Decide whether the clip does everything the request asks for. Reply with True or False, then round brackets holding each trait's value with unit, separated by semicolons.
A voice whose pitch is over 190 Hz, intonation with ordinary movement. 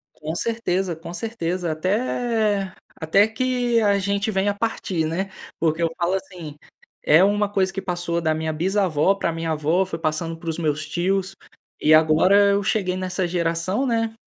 False (185 Hz; 3.5 semitones)